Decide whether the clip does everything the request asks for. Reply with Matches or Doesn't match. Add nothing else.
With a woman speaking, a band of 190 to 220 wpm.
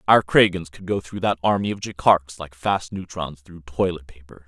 Doesn't match